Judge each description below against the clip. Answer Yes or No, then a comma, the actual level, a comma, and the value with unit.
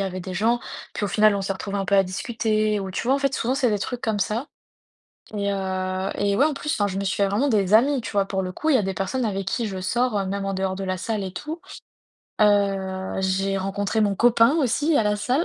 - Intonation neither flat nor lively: Yes, average, 3.3 semitones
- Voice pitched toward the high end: Yes, high, 205 Hz